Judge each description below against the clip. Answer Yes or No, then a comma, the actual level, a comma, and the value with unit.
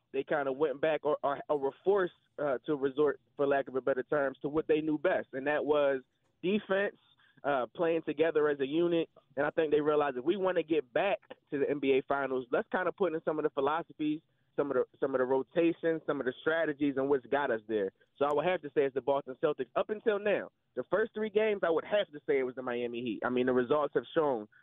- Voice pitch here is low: No, medium, 150 Hz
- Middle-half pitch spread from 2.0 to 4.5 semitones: Yes, average, 3.5 semitones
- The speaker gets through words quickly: Yes, fast, 260 wpm